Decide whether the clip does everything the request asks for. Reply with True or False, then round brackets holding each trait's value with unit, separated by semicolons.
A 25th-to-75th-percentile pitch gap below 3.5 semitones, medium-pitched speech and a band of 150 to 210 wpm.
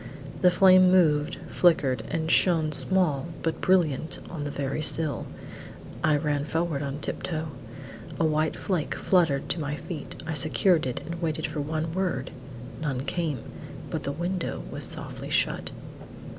True (2.9 semitones; 155 Hz; 155 wpm)